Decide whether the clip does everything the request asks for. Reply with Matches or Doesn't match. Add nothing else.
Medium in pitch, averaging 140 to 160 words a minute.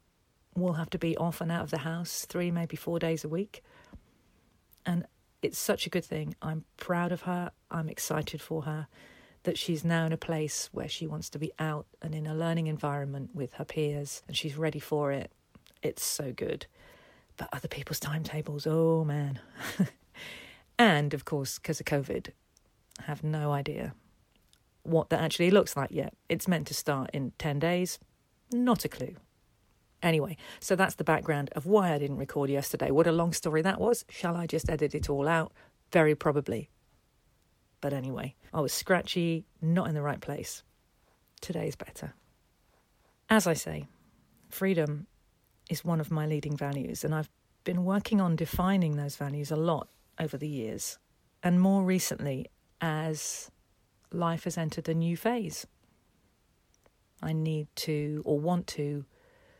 Doesn't match